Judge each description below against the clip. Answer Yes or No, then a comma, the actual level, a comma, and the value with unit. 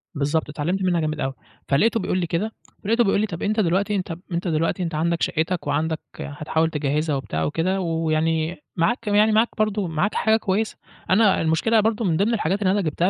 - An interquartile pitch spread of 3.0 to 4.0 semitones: No, average, 4.6 semitones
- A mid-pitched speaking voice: Yes, medium, 175 Hz